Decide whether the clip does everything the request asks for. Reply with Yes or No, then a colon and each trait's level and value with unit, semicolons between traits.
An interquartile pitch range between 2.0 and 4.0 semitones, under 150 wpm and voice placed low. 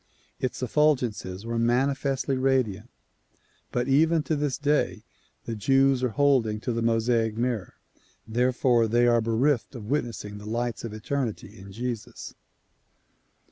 Yes: average, 3.2 semitones; slow, 135 wpm; low, 120 Hz